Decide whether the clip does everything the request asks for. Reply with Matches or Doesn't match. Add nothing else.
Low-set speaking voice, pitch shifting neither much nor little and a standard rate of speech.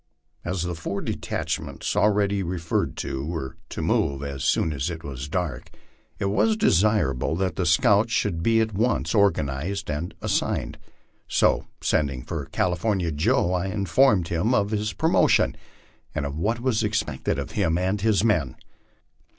Matches